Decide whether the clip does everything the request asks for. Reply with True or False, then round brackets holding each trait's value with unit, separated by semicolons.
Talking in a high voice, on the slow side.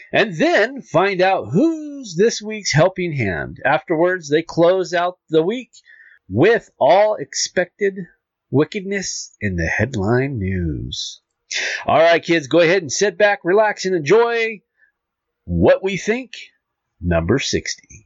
False (180 Hz; 130 wpm)